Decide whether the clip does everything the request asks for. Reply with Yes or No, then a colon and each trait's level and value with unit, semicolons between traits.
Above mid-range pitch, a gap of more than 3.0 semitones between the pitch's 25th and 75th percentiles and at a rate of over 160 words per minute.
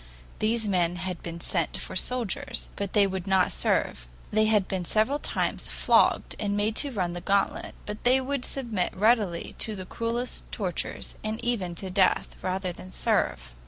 Yes: high, 200 Hz; average, 3.5 semitones; average, 175 wpm